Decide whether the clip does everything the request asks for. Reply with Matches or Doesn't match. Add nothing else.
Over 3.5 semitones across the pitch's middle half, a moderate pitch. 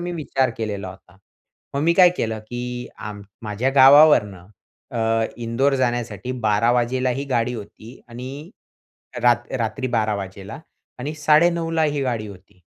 Doesn't match